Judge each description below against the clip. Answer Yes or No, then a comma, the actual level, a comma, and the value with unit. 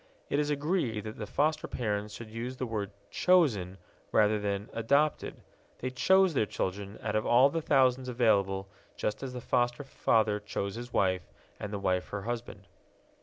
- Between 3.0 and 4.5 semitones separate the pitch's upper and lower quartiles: Yes, average, 4.2 semitones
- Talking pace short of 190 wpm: Yes, average, 170 wpm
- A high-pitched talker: No, low, 115 Hz